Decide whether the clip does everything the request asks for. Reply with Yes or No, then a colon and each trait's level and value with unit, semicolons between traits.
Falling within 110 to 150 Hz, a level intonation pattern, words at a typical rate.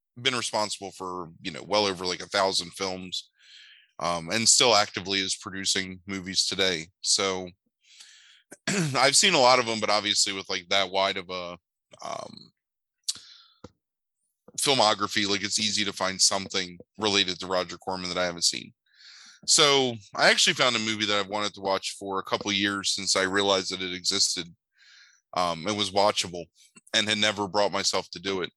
No: very low, 95 Hz; narrow, 2.1 semitones; average, 175 wpm